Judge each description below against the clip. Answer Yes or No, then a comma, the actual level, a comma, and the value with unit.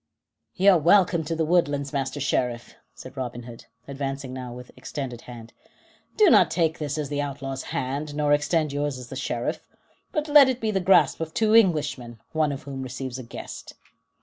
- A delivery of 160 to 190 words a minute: Yes, average, 185 wpm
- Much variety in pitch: No, average, 3.9 semitones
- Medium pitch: Yes, medium, 145 Hz